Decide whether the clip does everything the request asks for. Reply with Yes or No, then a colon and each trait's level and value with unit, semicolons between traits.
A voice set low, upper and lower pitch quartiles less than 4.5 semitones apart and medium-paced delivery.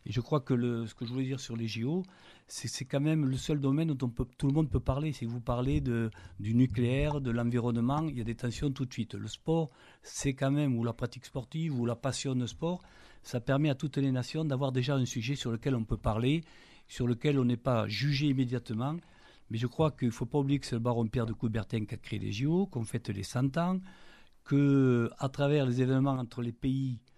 No: low, 130 Hz; average, 3.1 semitones; fast, 250 wpm